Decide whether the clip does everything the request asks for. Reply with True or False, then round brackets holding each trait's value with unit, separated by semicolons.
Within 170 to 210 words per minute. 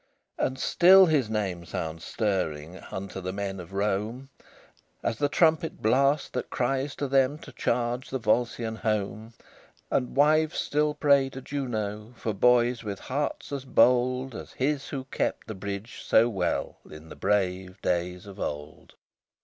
False (155 wpm)